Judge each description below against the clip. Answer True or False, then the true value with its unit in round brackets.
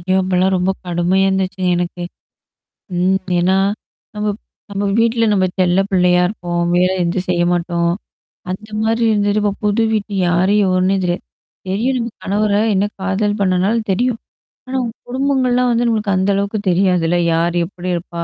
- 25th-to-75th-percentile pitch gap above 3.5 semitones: False (3.0 semitones)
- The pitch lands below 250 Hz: True (190 Hz)